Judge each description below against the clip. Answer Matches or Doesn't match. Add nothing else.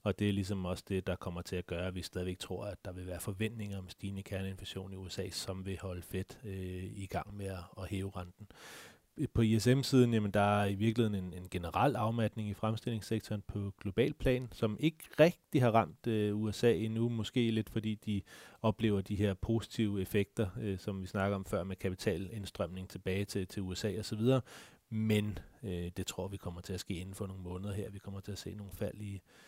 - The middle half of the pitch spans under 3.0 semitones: Matches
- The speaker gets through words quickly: Doesn't match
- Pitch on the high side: Doesn't match